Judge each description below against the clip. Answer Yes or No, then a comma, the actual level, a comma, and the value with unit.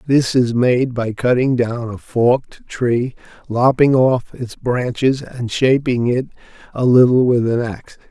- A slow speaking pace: No, average, 155 wpm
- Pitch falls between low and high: No, low, 125 Hz